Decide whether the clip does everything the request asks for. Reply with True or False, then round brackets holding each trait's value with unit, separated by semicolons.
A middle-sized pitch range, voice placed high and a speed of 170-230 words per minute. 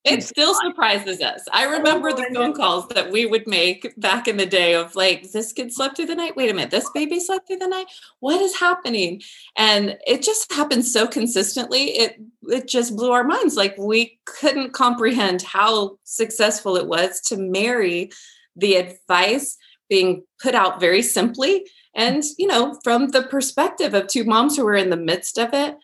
False (6.8 semitones; 235 Hz; 190 wpm)